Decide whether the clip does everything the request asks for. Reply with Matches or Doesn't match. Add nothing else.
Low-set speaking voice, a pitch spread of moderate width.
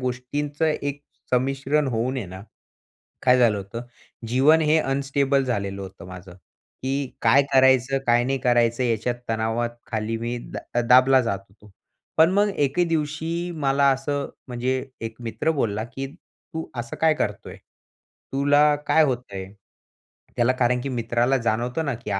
Matches